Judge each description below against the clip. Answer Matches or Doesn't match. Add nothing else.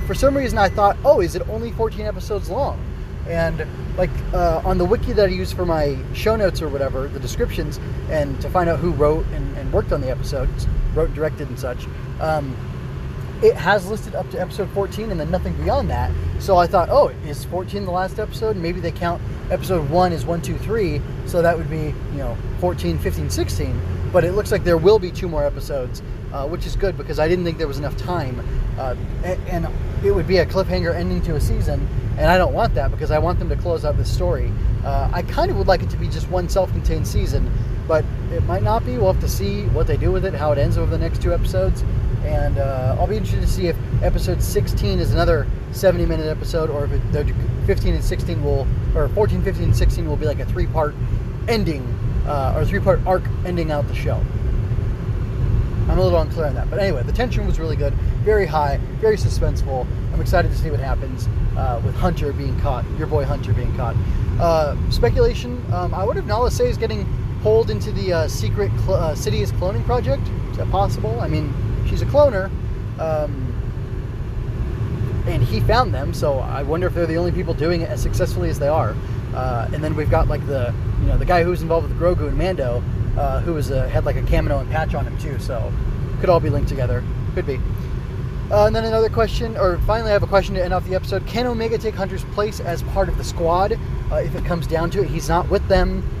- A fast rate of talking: Matches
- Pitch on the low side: Matches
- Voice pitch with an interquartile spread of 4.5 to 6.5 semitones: Matches